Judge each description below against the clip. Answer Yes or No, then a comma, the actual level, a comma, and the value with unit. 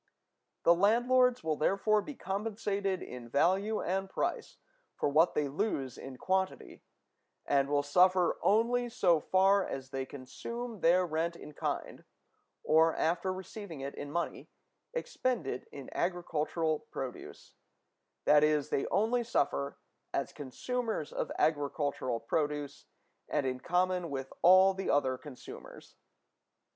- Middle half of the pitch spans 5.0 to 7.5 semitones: Yes, wide, 5.5 semitones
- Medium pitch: Yes, medium, 170 Hz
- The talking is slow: Yes, slow, 130 wpm